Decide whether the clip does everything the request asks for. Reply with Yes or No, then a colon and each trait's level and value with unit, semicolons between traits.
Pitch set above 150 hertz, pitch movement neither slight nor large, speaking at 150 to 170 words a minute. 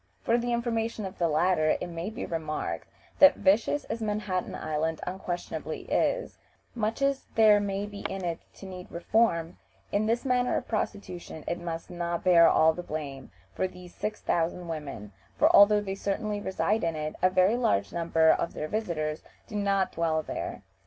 No: medium, 185 Hz; average, 4.3 semitones; average, 180 wpm